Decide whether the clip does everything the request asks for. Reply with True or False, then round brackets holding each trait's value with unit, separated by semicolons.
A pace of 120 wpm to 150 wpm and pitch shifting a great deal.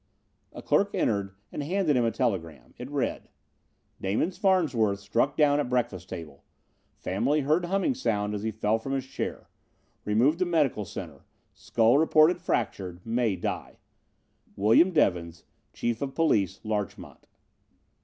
True (140 wpm; 7.0 semitones)